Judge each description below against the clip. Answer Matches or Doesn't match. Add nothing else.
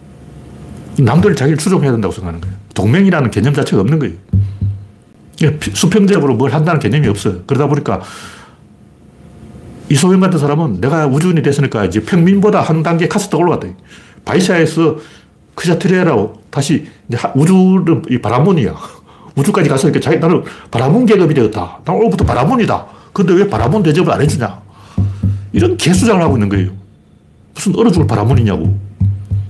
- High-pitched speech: Doesn't match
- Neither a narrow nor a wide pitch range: Doesn't match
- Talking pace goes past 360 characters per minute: Matches